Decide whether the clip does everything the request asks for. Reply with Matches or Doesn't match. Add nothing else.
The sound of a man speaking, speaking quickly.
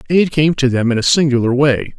Matches